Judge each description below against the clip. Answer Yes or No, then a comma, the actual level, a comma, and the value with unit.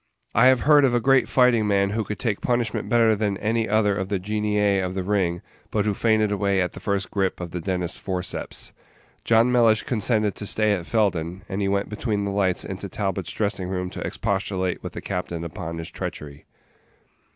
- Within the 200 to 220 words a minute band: Yes, fast, 205 wpm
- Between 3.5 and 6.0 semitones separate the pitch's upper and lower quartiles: No, average, 2.7 semitones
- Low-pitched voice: Yes, low, 100 Hz